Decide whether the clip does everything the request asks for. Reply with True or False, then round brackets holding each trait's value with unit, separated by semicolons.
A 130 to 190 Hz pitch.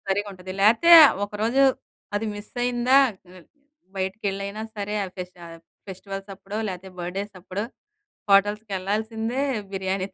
False (200 Hz)